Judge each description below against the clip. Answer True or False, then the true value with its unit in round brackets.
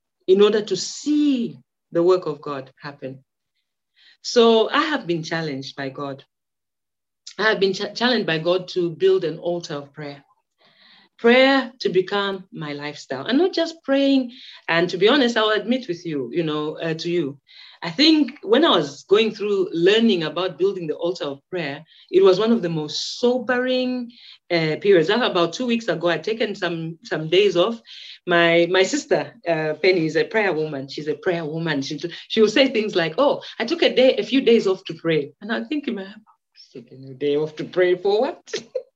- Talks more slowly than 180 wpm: False (195 wpm)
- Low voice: False (185 Hz)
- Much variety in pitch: True (6.9 semitones)